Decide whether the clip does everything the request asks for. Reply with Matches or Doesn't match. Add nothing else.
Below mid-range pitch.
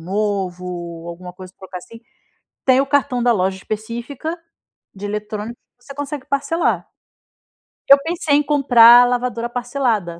Doesn't match